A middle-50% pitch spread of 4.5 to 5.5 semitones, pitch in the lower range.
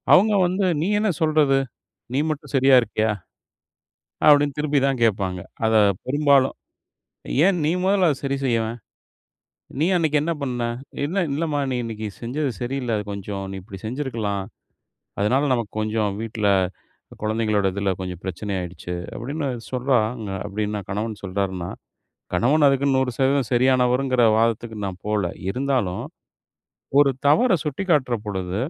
Yes: average, 5.2 semitones; low, 125 Hz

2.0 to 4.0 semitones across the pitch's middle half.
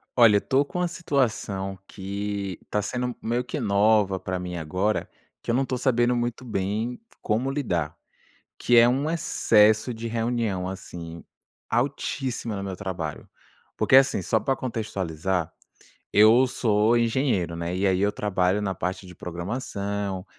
No: average, 4.4 semitones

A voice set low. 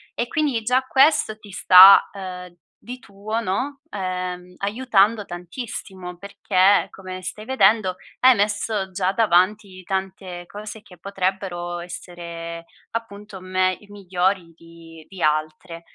No: high, 190 Hz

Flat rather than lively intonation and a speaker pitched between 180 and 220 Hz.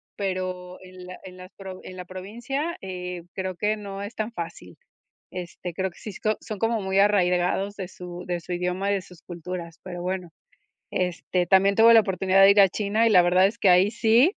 Yes: narrow, 2.2 semitones; medium, 185 Hz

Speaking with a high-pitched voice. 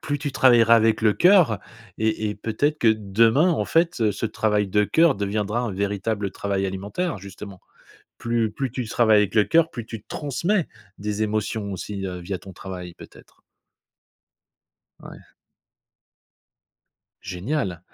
No: low, 110 Hz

